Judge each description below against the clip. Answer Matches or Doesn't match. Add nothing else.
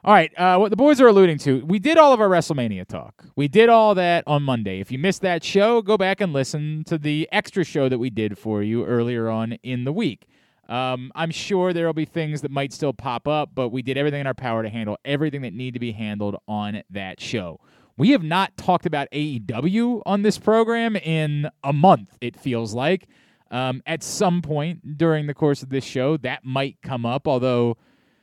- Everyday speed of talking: Doesn't match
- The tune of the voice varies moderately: Doesn't match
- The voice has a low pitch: Doesn't match